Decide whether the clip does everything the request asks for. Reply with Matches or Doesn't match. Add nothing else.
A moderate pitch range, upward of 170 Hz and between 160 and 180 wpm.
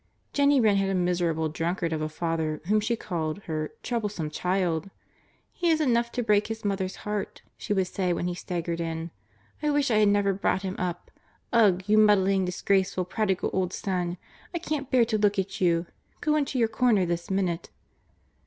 Doesn't match